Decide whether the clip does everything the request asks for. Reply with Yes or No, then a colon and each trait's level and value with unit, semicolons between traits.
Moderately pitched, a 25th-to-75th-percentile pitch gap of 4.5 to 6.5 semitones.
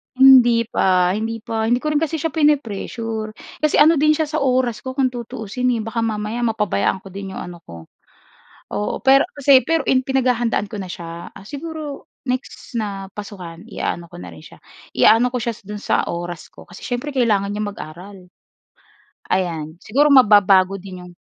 No: high, 225 Hz; average, 5.2 semitones